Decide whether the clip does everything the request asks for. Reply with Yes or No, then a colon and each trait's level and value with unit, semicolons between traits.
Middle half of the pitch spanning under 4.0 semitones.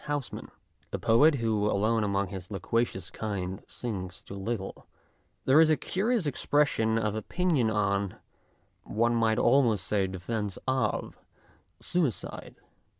No: average, 4.8 semitones